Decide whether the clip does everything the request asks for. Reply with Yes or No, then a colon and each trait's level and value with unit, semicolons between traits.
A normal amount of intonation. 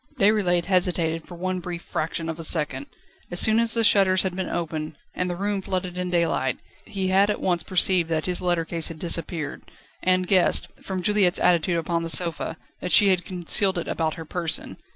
No: narrow, 2.1 semitones